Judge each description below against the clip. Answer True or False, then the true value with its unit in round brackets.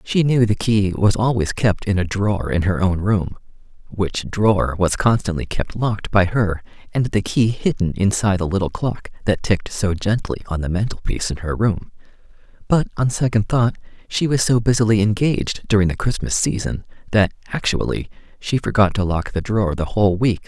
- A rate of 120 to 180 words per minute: False (190 wpm)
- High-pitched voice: False (105 Hz)